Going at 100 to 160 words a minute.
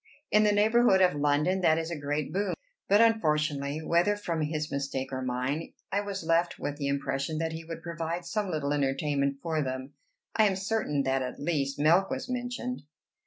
No: average, 190 wpm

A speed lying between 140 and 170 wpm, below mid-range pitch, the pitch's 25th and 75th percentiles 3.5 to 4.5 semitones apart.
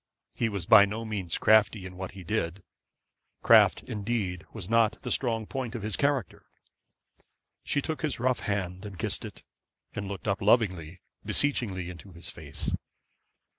Yes: average, 160 wpm; low, 100 Hz; average, 3.8 semitones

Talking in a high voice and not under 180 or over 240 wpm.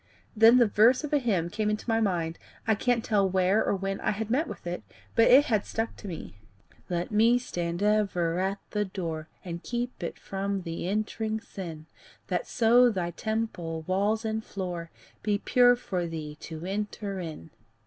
Yes: high, 200 Hz; average, 185 wpm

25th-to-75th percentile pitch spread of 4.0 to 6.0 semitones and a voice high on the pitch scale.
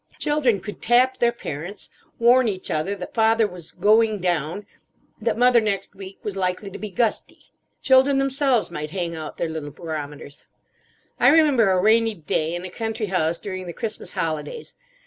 Yes: average, 5.3 semitones; high, 200 Hz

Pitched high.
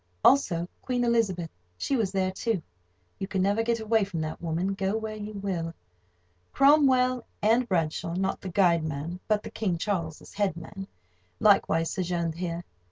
Yes: high, 195 Hz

